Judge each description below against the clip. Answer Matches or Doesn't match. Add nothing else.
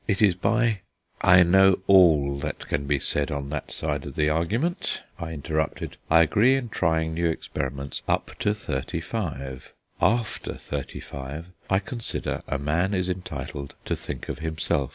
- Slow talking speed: Doesn't match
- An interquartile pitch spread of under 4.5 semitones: Doesn't match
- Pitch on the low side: Matches